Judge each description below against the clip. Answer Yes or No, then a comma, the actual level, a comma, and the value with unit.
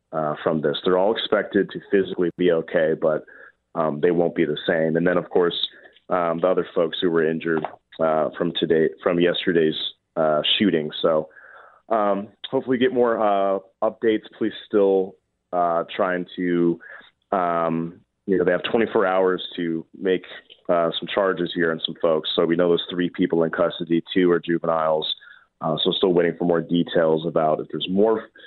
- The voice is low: Yes, very low, 85 Hz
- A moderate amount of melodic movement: No, narrow, 2.3 semitones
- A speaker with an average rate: Yes, average, 180 wpm